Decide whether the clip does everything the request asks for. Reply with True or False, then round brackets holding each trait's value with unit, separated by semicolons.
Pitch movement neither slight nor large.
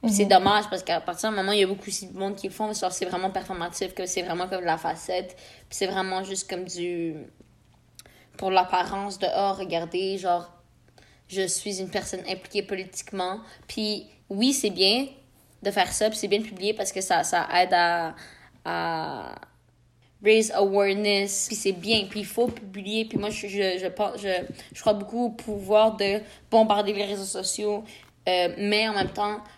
False (2.1 semitones)